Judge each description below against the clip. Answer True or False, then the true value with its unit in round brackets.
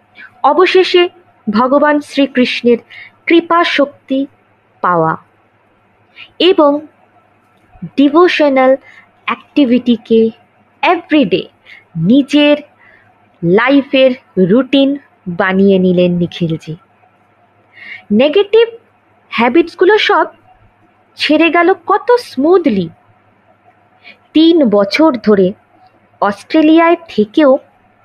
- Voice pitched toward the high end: True (275 Hz)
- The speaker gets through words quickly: False (60 wpm)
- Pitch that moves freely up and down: True (7.9 semitones)